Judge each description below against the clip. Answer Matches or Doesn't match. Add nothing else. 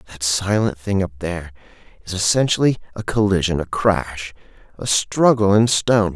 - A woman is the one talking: Doesn't match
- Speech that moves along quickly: Doesn't match